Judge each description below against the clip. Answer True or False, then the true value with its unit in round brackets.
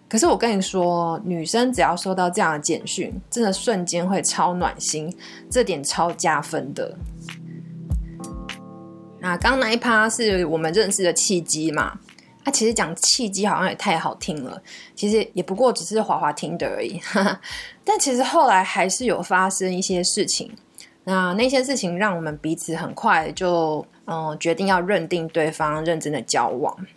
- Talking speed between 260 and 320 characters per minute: False (250 characters per minute)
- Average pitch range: True (4.9 semitones)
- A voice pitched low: False (185 Hz)